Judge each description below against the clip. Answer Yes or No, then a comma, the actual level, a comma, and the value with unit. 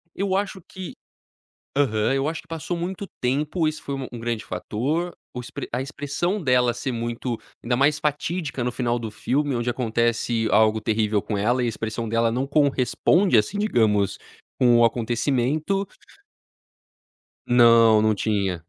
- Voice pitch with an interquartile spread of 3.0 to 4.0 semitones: No, average, 4.6 semitones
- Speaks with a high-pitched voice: No, low, 125 Hz